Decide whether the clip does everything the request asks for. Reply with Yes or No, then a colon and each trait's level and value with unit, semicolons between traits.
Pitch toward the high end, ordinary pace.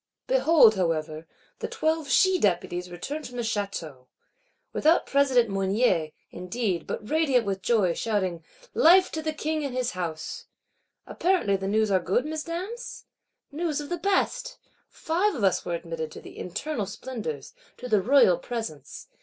Yes: high, 225 Hz; average, 155 wpm